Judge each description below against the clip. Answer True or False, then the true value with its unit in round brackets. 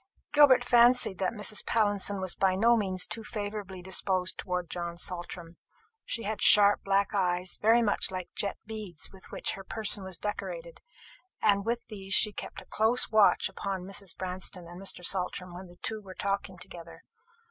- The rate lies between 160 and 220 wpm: True (180 wpm)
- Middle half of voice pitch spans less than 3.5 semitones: True (2.7 semitones)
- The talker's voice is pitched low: False (195 Hz)